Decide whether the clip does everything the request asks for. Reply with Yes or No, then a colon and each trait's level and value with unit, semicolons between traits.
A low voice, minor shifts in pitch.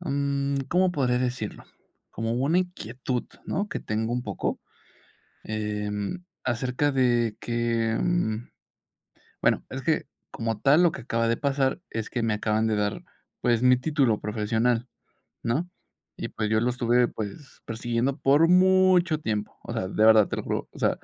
No: low, 120 Hz; average, 4.0 semitones